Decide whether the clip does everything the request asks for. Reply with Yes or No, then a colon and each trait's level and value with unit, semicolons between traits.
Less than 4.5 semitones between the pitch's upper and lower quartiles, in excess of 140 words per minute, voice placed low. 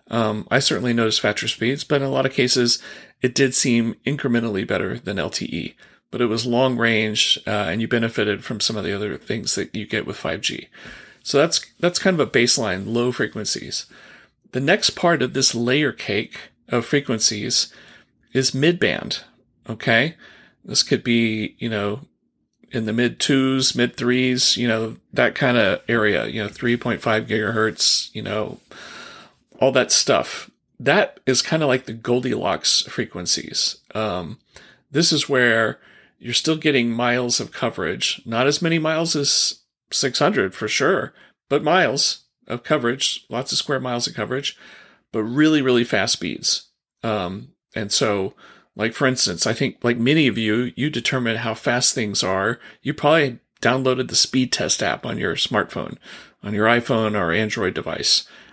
Yes: average, 2.9 semitones; average, 170 wpm; low, 120 Hz